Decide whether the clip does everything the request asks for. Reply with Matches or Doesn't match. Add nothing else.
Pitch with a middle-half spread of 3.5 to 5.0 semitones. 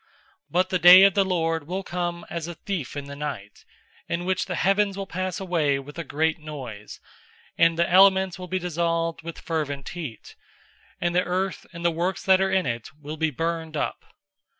Doesn't match